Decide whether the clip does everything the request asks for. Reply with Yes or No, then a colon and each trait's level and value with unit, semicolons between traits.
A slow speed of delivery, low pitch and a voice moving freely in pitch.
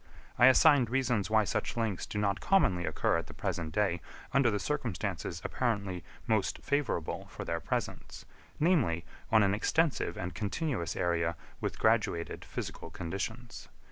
No: average, 145 wpm; low, 105 Hz; wide, 6.1 semitones